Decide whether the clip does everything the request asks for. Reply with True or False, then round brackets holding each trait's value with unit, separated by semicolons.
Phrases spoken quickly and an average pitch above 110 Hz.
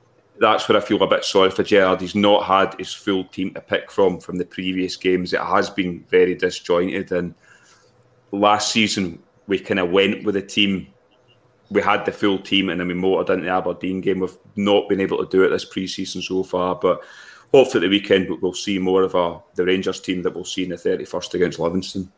False (220 wpm; 95 Hz)